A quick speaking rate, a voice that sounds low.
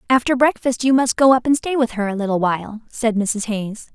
No: fast, 245 wpm; high, 235 Hz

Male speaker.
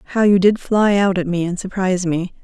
No: female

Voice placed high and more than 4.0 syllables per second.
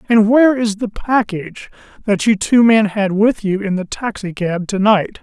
Yes: high, 210 Hz; 4.7 syllables/s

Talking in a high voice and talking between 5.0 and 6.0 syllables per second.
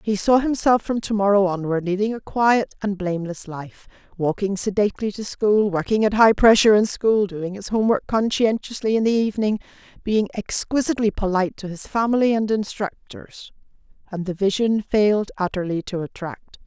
Yes: high, 205 Hz; 5.4 syllables/s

